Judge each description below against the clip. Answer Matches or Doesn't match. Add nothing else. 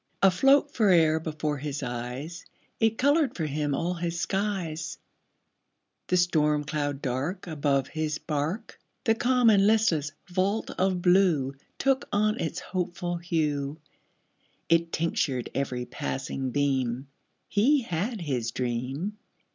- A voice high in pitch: Doesn't match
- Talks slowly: Matches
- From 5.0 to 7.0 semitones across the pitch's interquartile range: Matches